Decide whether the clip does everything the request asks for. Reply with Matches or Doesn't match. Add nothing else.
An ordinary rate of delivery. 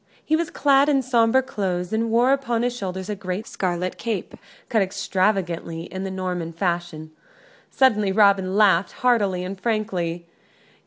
Matches